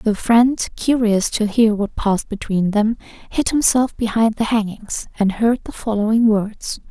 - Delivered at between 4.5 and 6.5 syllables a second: No, 4.3 syllables/s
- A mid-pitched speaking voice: No, high, 220 Hz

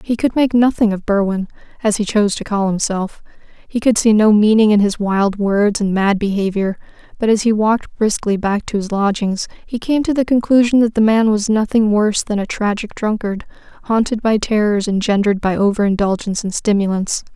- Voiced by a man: No, female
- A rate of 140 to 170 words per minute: No, average, 190 wpm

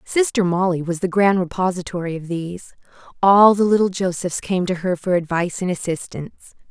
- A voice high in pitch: No, medium, 180 Hz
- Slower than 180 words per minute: Yes, average, 170 wpm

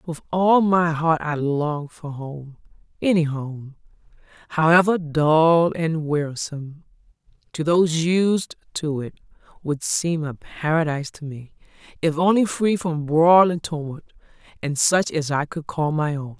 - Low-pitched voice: No, medium, 160 Hz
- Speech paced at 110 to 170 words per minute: Yes, average, 145 wpm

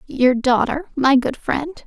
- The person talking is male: No, female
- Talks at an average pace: Yes, average, 160 wpm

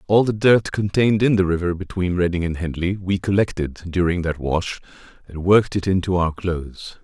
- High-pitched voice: No, very low, 90 Hz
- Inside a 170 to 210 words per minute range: Yes, average, 190 wpm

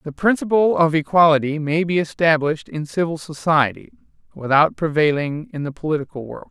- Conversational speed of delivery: Yes, average, 150 wpm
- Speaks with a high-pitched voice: No, medium, 160 Hz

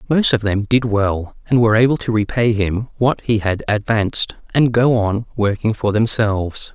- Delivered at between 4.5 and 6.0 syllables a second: Yes, 4.9 syllables/s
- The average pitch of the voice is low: Yes, low, 110 Hz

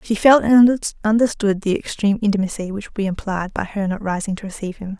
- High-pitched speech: Yes, high, 205 Hz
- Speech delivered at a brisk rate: Yes, fast, 215 wpm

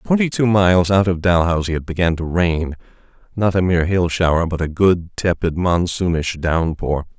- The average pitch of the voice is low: Yes, very low, 90 Hz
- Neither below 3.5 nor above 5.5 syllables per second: Yes, 5.1 syllables/s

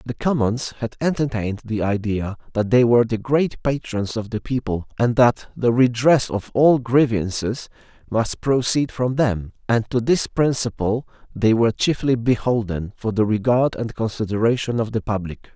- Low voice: Yes, low, 115 Hz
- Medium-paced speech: Yes, average, 160 wpm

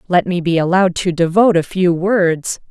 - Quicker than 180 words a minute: Yes, average, 200 wpm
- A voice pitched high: No, medium, 180 Hz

